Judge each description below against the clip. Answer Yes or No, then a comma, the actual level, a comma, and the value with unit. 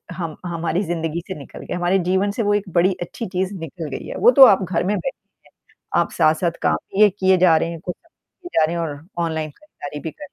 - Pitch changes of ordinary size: Yes, average, 3.3 semitones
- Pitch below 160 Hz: No, medium, 175 Hz